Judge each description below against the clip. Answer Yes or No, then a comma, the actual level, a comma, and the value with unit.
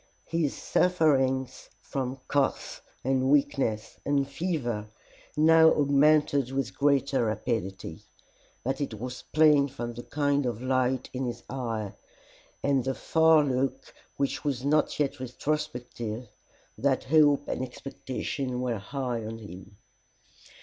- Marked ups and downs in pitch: No, average, 2.9 semitones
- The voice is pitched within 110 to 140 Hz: Yes, low, 135 Hz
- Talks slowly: Yes, slow, 120 wpm